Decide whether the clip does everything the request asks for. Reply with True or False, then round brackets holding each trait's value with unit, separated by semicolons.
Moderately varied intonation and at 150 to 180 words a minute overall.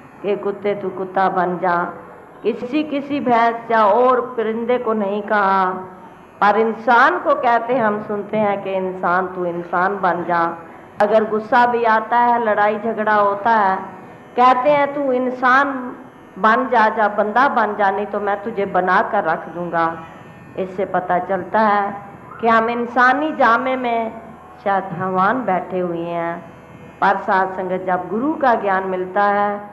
True (3.8 semitones; 155 wpm)